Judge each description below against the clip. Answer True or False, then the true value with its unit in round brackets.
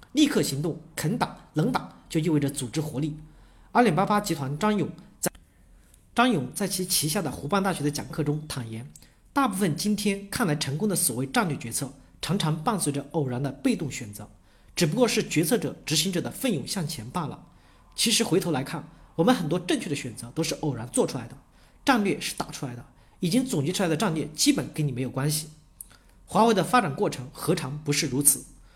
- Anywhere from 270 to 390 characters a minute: True (305 characters per minute)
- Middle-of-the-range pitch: True (155 Hz)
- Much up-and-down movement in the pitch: True (5.9 semitones)